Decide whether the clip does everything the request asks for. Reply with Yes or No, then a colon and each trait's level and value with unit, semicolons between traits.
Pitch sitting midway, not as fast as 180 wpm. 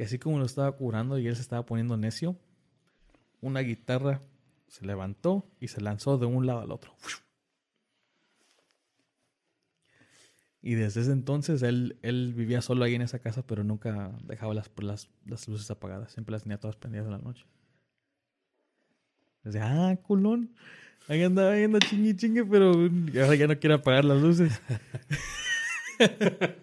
No: low, 130 Hz; average, 155 wpm